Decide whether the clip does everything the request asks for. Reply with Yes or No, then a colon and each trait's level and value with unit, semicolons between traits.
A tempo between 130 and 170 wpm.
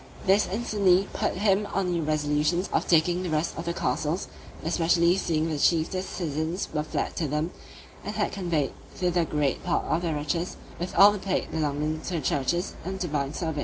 No: average, 190 wpm